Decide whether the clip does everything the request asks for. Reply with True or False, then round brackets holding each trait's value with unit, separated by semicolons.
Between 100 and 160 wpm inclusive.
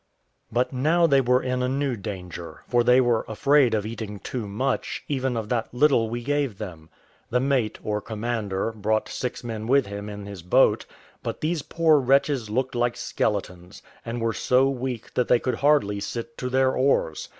False (185 wpm)